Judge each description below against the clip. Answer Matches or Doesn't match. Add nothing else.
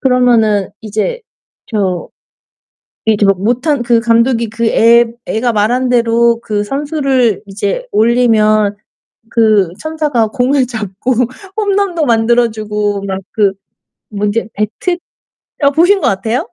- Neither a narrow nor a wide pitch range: Matches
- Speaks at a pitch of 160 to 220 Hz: Doesn't match